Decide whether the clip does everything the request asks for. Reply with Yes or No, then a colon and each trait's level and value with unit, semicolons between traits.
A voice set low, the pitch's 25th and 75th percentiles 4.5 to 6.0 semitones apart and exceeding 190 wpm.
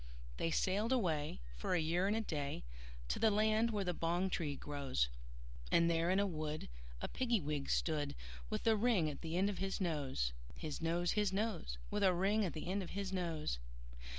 No: medium, 175 Hz; average, 4.8 semitones; fast, 205 wpm